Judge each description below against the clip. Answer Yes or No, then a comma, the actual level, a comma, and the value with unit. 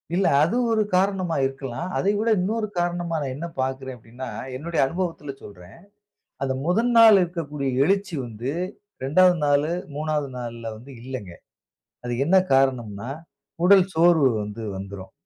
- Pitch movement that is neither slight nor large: No, wide, 5.9 semitones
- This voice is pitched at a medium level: Yes, medium, 145 Hz